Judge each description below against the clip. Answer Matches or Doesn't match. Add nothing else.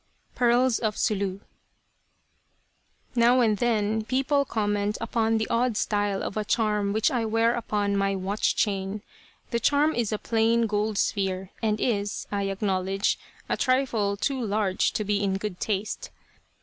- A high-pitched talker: Matches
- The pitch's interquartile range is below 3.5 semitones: Matches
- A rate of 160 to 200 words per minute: Doesn't match